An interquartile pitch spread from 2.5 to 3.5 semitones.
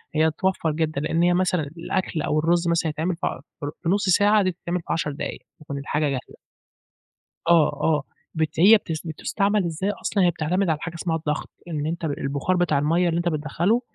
Yes: average, 2.8 semitones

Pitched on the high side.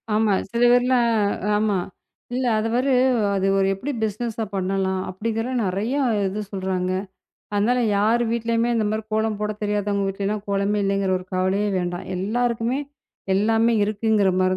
Yes: high, 210 Hz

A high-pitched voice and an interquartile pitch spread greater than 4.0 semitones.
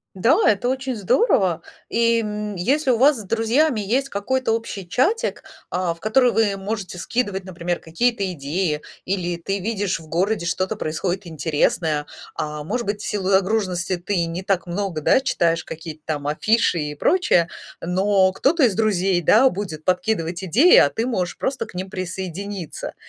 Yes: high, 195 Hz; average, 4.5 semitones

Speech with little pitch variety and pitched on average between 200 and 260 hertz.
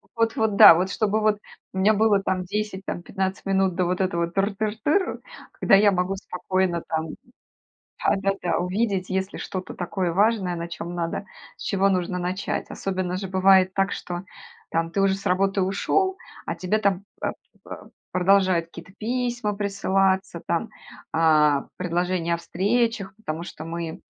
No: narrow, 2.2 semitones; high, 190 Hz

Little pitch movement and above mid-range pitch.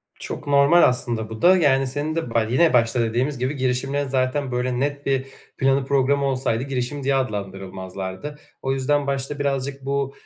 No: narrow, 2.3 semitones; low, 135 Hz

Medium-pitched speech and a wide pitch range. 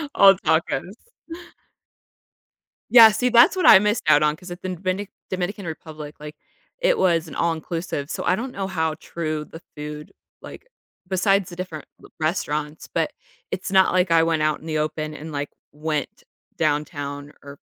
No: medium, 165 Hz; average, 3.7 semitones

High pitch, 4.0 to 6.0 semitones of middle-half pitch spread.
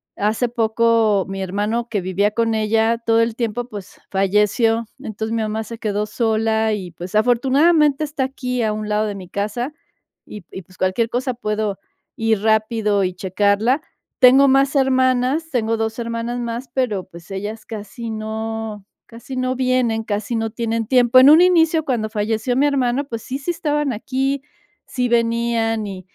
No: high, 225 Hz; average, 3.0 semitones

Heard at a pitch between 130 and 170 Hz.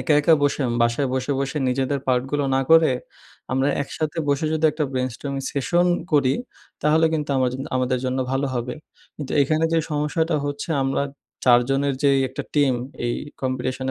Yes: medium, 140 Hz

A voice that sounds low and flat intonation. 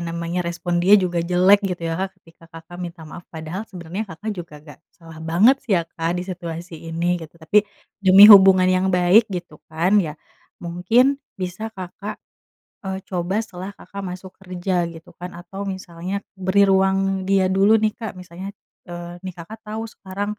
No: medium, 180 Hz; narrow, 2.2 semitones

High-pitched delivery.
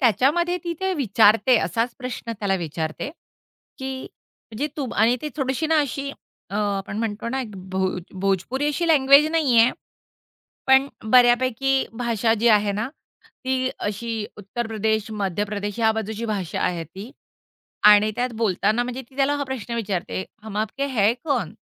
Yes: high, 230 Hz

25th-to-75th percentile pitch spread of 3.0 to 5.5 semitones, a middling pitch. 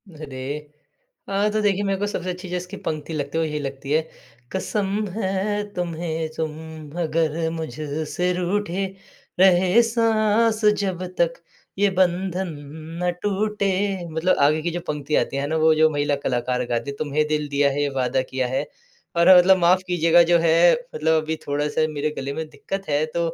Yes: average, 4.1 semitones; medium, 170 Hz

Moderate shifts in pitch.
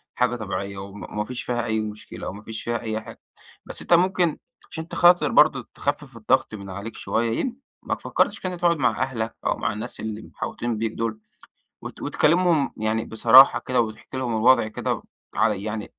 Yes: average, 3.3 semitones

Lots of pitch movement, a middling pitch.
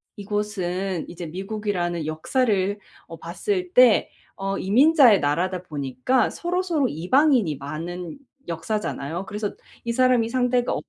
No: wide, 6.3 semitones; high, 195 Hz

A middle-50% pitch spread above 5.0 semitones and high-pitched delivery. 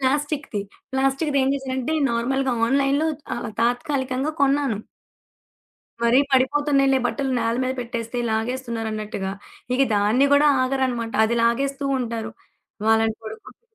No: average, 2.9 semitones; very high, 260 Hz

